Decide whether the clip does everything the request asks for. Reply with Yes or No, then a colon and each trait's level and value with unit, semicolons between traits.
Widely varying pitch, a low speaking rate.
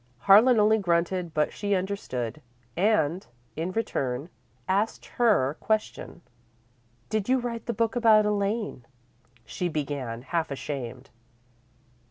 Yes: wide, 6.5 semitones; slow, 115 wpm